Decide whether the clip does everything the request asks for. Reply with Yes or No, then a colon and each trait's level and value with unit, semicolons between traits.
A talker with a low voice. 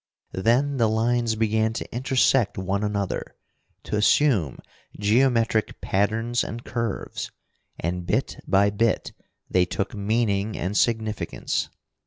Yes: low, 110 Hz